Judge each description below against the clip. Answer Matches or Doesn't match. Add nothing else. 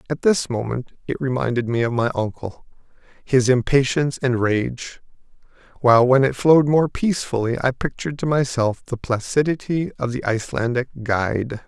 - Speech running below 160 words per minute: Matches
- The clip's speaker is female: Doesn't match